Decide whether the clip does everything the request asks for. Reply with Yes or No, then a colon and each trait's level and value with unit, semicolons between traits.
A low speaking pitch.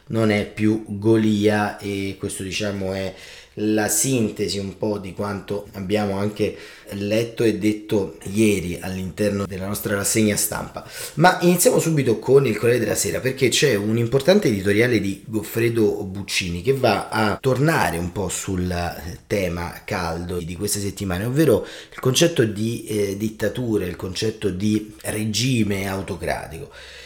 Yes: low, 105 Hz